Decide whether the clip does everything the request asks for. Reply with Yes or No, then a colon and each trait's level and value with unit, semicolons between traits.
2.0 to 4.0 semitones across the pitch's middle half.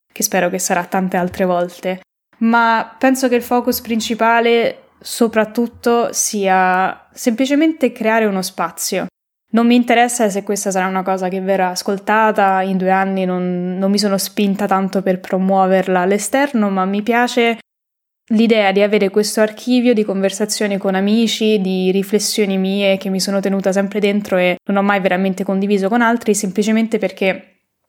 Yes: average, 3.1 semitones